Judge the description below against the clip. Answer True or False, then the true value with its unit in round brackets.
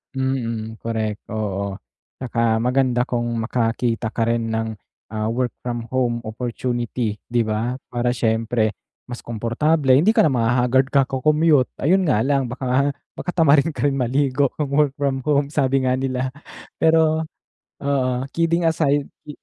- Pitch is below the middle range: True (125 Hz)